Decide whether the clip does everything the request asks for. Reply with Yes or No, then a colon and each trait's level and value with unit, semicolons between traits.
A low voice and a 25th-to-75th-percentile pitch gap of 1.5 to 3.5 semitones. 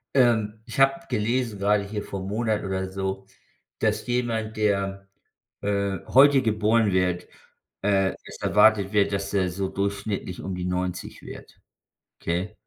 Yes: low, 100 Hz; narrow, 2.4 semitones